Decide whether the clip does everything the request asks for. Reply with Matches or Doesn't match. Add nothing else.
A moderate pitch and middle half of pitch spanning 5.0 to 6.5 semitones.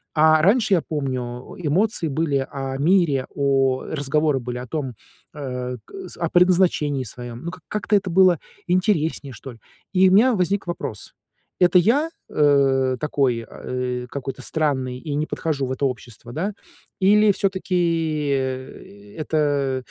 Matches